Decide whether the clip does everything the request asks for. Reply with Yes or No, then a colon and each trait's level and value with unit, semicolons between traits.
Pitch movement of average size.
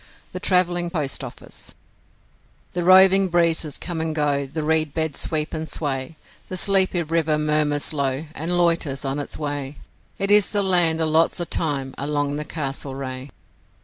Yes: average, 3.2 semitones